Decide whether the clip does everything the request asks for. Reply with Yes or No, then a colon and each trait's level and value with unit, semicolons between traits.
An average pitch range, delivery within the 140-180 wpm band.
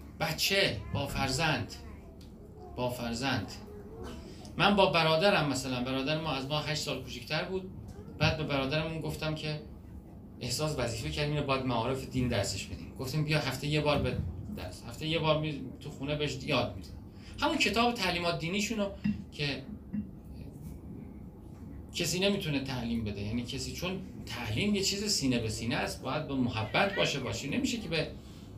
Yes: average, 4.8 semitones; fast, 155 wpm